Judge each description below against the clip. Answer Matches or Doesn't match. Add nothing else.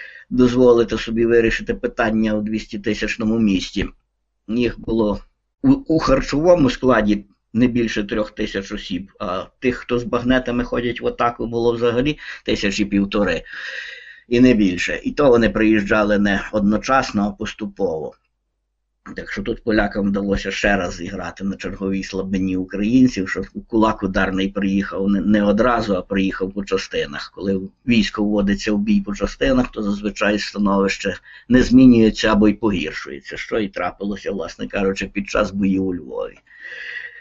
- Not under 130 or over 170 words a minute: Matches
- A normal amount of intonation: Matches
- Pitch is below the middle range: Matches